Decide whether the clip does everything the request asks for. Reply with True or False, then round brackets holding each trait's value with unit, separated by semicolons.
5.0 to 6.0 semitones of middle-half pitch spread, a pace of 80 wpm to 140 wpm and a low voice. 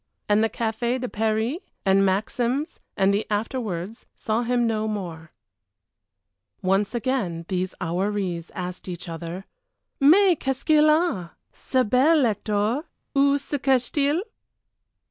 False (5.5 semitones; 135 wpm; 220 Hz)